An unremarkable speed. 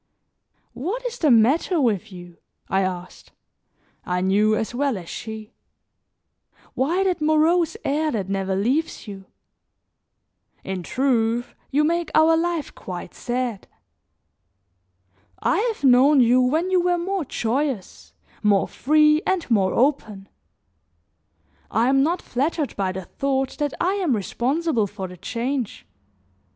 No: slow, 130 wpm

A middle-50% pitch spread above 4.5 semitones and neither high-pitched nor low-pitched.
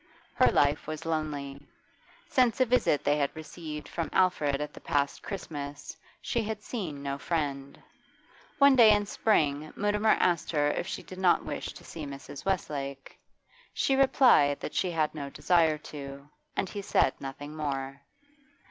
Yes: average, 5.1 semitones; medium, 155 Hz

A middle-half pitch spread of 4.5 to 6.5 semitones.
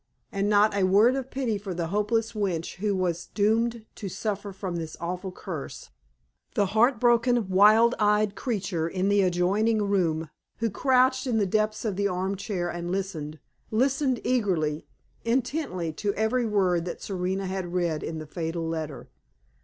No: average, 3.8 semitones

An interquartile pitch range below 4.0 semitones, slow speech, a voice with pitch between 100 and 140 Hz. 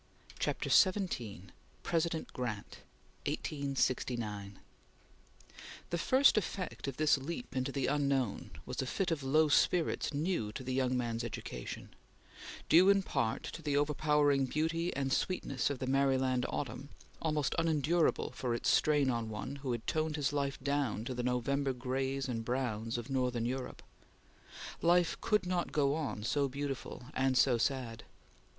No: average, 3.6 semitones; average, 150 wpm; low, 135 Hz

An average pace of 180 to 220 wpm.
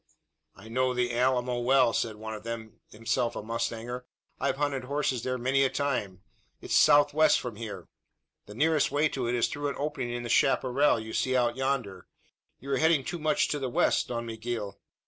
Yes: average, 195 wpm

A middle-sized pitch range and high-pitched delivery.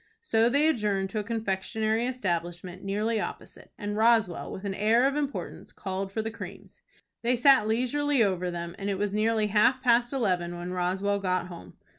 Yes: average, 3.7 semitones; high, 210 Hz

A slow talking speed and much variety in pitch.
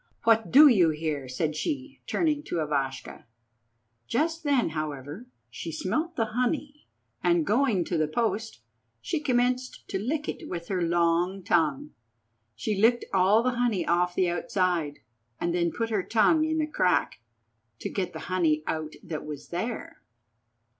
No: average, 155 wpm; wide, 7.3 semitones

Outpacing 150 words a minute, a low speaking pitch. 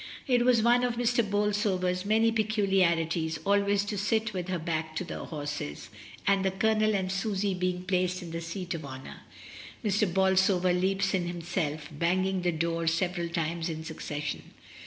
No: average, 165 wpm; medium, 185 Hz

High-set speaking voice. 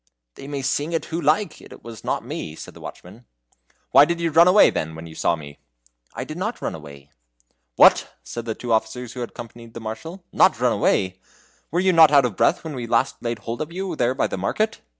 No: low, 125 Hz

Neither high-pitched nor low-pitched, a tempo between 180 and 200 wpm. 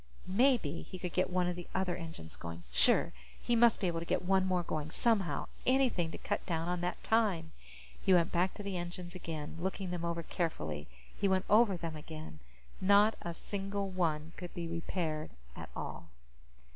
Yes: medium, 175 Hz; average, 190 wpm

